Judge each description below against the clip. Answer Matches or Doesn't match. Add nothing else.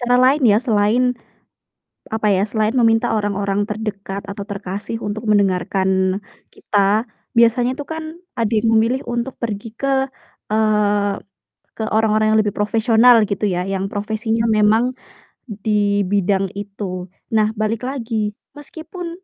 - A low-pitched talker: Doesn't match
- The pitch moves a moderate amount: Doesn't match